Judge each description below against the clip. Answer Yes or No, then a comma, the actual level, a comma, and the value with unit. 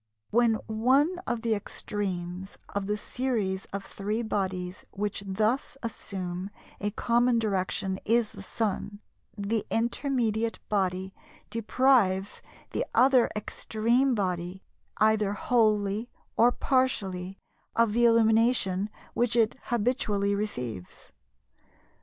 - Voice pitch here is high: Yes, high, 215 Hz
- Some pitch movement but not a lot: Yes, average, 3.3 semitones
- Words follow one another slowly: Yes, slow, 105 wpm